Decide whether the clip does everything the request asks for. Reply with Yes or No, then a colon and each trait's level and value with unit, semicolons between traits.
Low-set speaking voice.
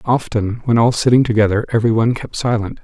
Yes: low, 115 Hz